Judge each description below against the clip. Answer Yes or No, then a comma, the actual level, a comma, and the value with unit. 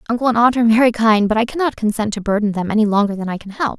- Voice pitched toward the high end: Yes, high, 220 Hz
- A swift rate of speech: Yes, fast, 300 wpm